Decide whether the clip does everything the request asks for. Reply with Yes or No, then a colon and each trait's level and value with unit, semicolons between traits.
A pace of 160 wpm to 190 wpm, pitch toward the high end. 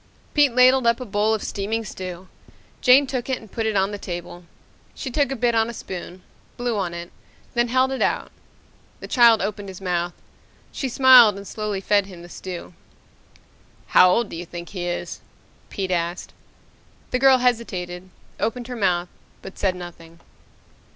Yes: average, 180 wpm; high, 205 Hz